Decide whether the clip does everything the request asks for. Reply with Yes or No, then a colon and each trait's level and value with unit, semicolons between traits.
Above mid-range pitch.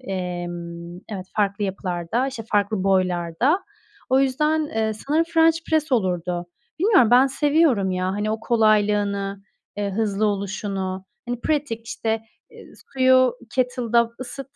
Yes: high, 215 Hz